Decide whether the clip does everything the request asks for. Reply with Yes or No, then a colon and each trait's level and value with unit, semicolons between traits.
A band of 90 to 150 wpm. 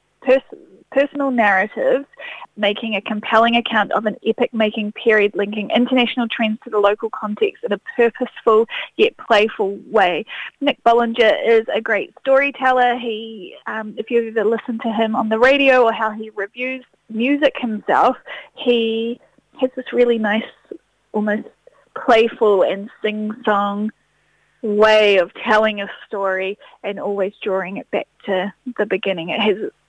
Yes: average, 145 wpm